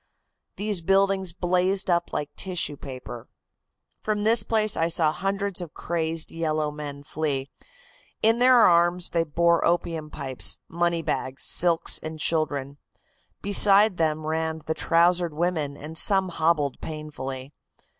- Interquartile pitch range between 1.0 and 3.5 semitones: Yes, average, 3.2 semitones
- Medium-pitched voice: Yes, medium, 165 Hz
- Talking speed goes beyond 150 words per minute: No, slow, 135 wpm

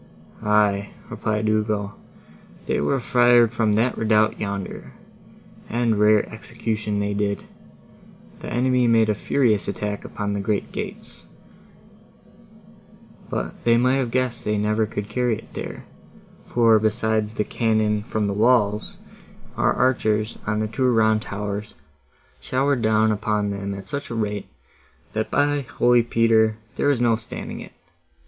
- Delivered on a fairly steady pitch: Yes, narrow, 2.1 semitones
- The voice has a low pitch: Yes, low, 110 Hz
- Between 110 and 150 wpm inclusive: Yes, average, 140 wpm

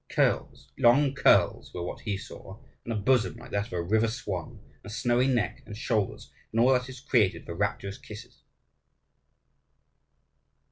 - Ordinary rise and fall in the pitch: Yes, average, 3.5 semitones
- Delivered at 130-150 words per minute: No, average, 170 wpm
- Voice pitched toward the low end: Yes, low, 110 Hz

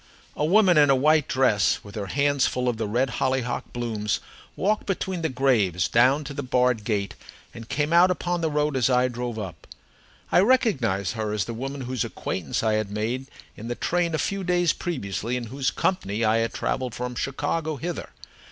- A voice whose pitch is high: No, low, 130 Hz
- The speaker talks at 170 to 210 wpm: Yes, average, 200 wpm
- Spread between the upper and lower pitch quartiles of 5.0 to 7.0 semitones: Yes, average, 5.3 semitones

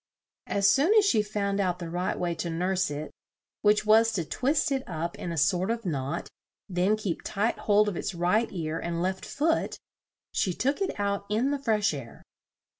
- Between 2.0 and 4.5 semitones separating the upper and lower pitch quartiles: Yes, average, 4.2 semitones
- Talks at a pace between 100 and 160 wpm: No, average, 195 wpm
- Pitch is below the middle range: No, high, 195 Hz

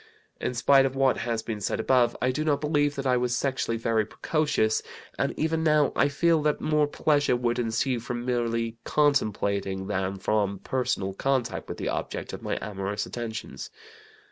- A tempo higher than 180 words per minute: No, average, 175 wpm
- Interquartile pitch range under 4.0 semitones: No, average, 4.4 semitones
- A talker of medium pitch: No, low, 120 Hz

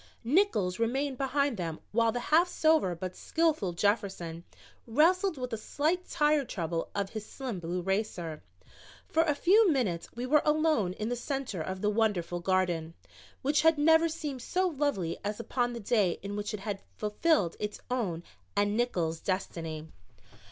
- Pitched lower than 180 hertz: No, high, 225 Hz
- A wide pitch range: Yes, wide, 7.8 semitones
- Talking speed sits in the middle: Yes, average, 165 wpm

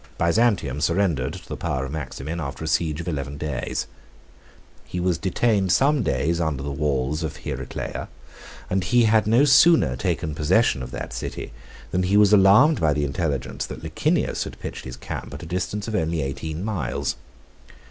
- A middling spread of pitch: No, wide, 5.7 semitones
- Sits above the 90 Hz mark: No, very low, 80 Hz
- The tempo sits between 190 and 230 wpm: No, average, 180 wpm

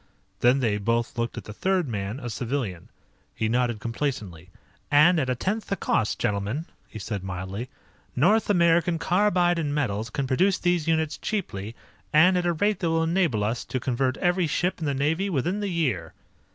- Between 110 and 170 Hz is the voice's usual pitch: Yes, medium, 140 Hz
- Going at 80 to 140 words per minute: No, average, 185 wpm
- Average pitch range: No, wide, 7.4 semitones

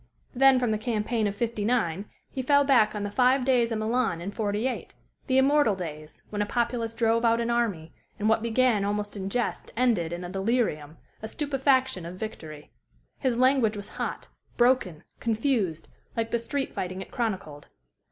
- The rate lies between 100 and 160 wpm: No, average, 175 wpm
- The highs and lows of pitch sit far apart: No, average, 4.0 semitones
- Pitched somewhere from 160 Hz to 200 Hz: No, high, 225 Hz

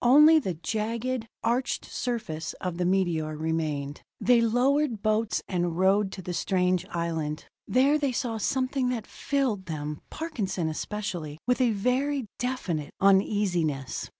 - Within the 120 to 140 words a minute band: Yes, slow, 135 wpm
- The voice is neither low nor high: No, high, 205 Hz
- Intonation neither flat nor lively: No, wide, 6.7 semitones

